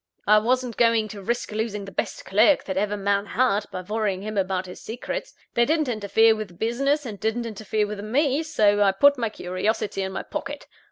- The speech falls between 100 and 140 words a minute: No, fast, 205 wpm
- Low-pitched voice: No, high, 215 Hz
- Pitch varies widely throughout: No, average, 2.9 semitones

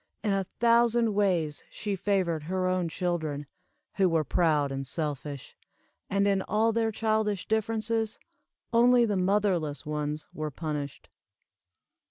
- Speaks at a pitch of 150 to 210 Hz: Yes, medium, 185 Hz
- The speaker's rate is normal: No, slow, 130 wpm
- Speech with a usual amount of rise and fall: No, wide, 6.0 semitones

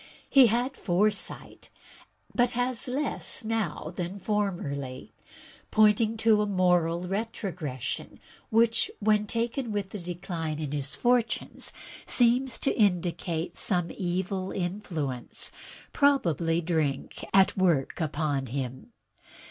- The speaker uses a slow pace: Yes, slow, 110 wpm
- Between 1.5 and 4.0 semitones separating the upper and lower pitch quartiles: No, wide, 5.5 semitones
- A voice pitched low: No, high, 190 Hz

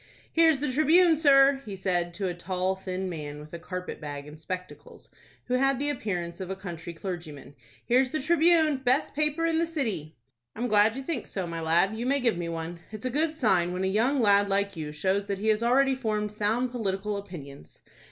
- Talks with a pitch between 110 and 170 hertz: No, high, 205 Hz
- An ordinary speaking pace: No, fast, 210 wpm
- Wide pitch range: Yes, wide, 7.3 semitones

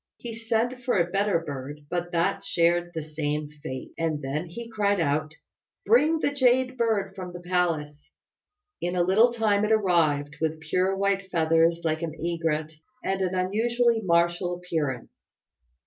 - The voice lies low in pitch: No, medium, 175 Hz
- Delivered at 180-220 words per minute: No, average, 160 wpm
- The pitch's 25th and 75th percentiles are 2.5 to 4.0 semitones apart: No, average, 4.8 semitones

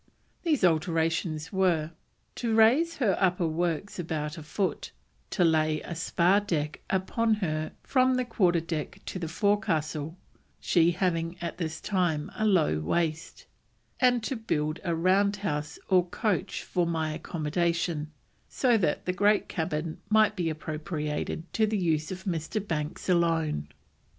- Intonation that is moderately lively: Yes, average, 4.1 semitones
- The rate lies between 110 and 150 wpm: Yes, average, 145 wpm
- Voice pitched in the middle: Yes, medium, 170 Hz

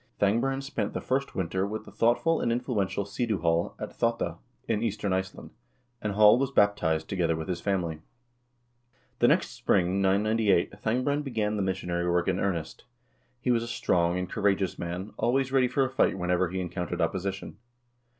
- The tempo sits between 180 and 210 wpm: No, average, 170 wpm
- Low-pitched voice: Yes, low, 100 Hz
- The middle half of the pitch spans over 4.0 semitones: Yes, average, 4.6 semitones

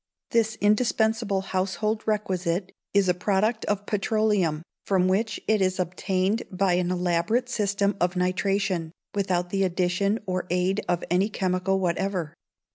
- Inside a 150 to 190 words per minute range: No, slow, 135 wpm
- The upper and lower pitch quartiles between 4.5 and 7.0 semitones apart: No, narrow, 2.4 semitones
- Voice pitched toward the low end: No, high, 190 Hz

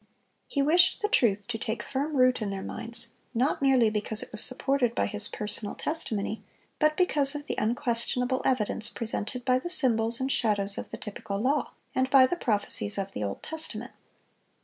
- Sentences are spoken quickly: No, average, 185 wpm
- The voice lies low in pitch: No, high, 240 Hz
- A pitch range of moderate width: Yes, average, 4.2 semitones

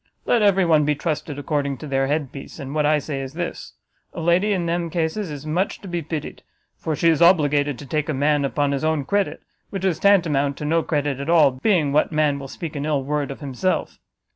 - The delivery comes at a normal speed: No, fast, 230 wpm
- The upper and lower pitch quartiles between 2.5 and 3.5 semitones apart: Yes, average, 3.1 semitones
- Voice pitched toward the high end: No, medium, 150 Hz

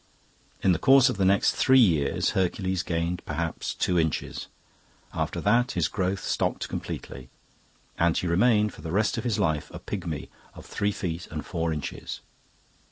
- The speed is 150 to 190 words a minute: Yes, average, 165 wpm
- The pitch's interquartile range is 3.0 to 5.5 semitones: Yes, average, 3.9 semitones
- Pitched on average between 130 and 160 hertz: No, very low, 90 Hz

